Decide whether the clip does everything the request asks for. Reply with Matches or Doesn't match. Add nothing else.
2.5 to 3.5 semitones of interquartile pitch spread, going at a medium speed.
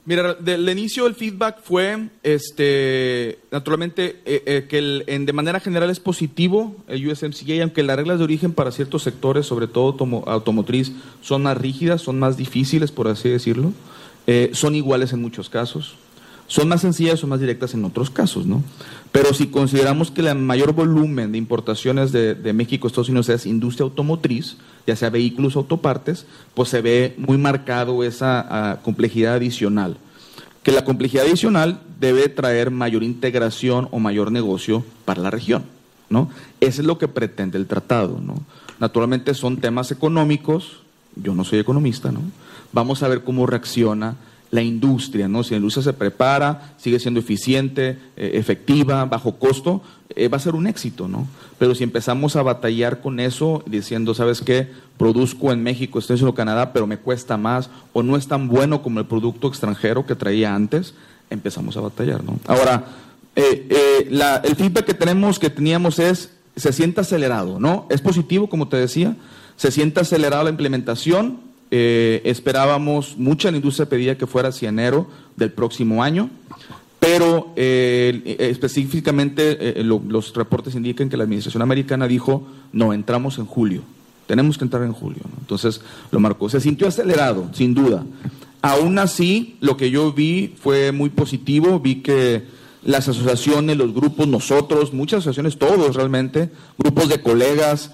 Doesn't match